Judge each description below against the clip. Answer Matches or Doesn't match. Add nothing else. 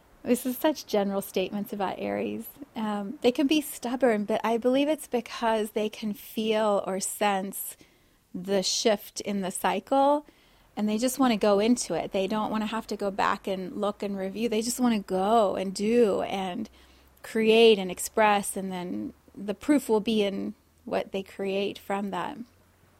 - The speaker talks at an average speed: Matches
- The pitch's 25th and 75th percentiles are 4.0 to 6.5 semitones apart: Doesn't match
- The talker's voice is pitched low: Doesn't match